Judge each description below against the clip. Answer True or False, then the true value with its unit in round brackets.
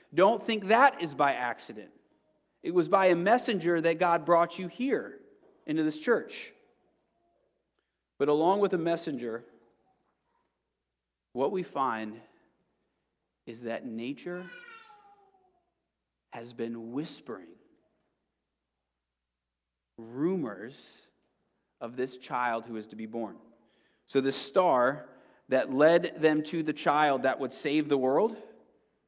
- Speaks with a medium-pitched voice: True (155 Hz)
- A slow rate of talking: True (115 wpm)